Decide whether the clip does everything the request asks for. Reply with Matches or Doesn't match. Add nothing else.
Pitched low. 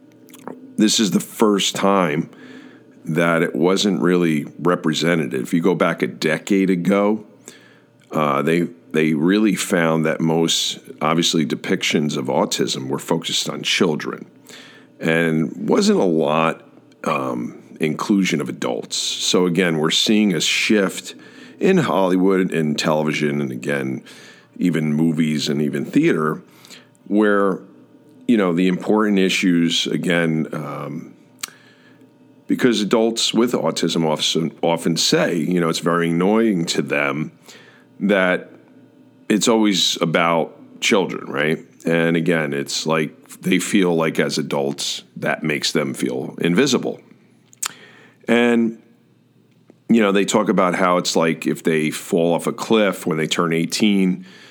Matches